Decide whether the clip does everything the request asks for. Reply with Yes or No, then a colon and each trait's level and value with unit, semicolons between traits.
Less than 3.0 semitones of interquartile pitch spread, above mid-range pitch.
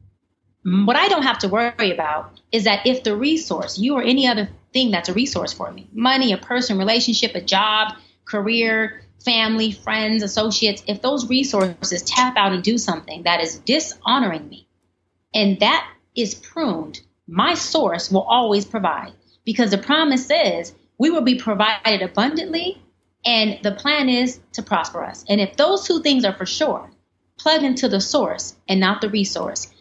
No: average, 4.5 semitones; high, 220 Hz